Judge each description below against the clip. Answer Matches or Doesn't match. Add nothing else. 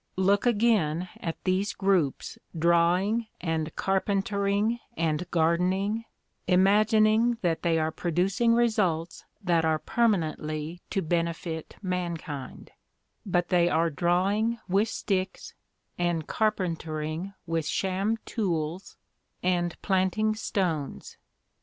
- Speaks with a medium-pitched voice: Matches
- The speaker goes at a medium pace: Doesn't match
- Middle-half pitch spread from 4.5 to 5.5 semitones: Doesn't match